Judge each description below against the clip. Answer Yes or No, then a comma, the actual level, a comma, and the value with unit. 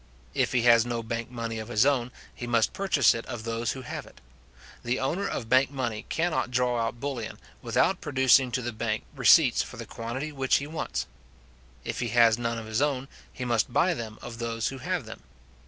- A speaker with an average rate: No, fast, 210 wpm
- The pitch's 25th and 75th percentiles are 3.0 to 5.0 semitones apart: No, narrow, 2.5 semitones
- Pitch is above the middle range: No, low, 120 Hz